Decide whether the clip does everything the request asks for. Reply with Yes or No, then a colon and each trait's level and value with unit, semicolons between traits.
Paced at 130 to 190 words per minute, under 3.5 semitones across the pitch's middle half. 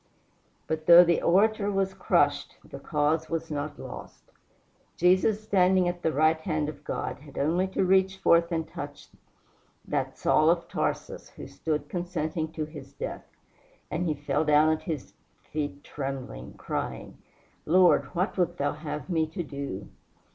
Yes: average, 155 wpm; average, 2.9 semitones